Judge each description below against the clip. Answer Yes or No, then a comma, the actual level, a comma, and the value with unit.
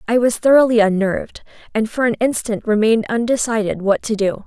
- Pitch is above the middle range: Yes, high, 225 Hz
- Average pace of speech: Yes, average, 175 wpm